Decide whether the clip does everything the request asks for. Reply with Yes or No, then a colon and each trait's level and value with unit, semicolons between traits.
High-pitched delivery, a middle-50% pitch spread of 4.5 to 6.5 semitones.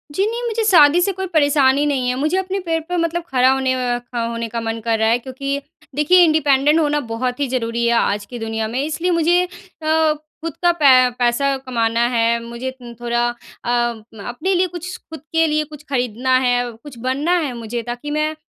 Yes: very high, 265 Hz; average, 5.0 semitones